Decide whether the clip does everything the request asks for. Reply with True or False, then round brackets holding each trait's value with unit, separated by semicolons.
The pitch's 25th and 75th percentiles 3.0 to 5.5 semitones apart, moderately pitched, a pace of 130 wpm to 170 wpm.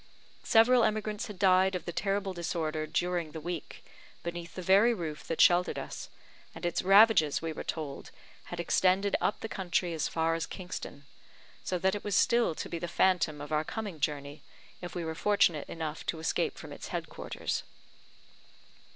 False (3.4 semitones; 175 Hz; 180 wpm)